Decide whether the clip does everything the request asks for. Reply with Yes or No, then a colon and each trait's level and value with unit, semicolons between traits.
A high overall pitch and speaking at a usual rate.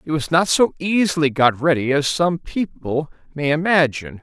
No: medium, 155 Hz; average, 170 wpm